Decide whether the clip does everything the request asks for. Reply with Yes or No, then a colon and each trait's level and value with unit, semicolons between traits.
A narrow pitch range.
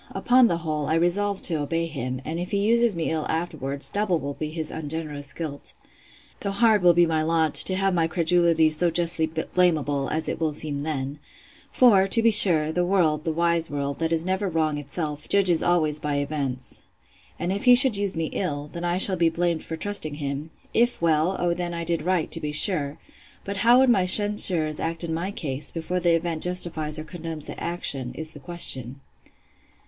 No: average, 3.0 semitones